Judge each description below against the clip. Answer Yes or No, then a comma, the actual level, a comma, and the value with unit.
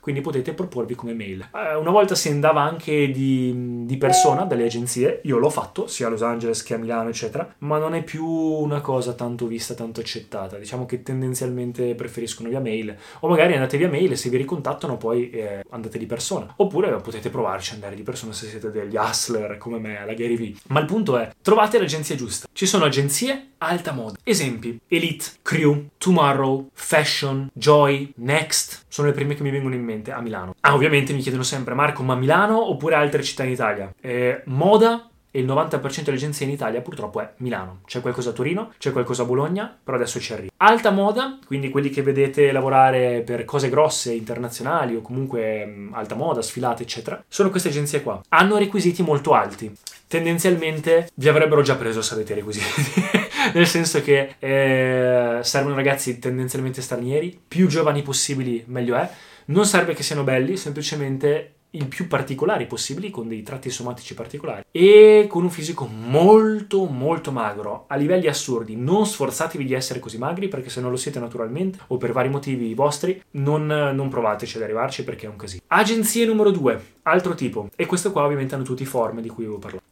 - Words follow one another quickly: Yes, fast, 190 wpm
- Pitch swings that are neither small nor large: Yes, average, 4.8 semitones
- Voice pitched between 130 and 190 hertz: Yes, low, 135 Hz